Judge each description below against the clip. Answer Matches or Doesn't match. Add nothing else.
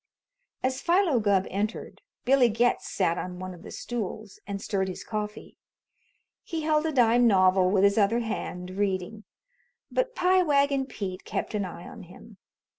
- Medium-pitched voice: Doesn't match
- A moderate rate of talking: Matches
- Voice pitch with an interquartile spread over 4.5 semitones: Matches